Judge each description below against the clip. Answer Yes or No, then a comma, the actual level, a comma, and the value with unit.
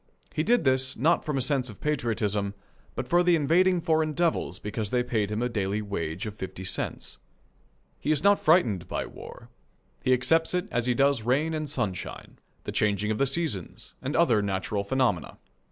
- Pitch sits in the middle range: No, low, 125 Hz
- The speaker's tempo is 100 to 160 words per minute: No, average, 185 wpm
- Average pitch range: No, wide, 6.9 semitones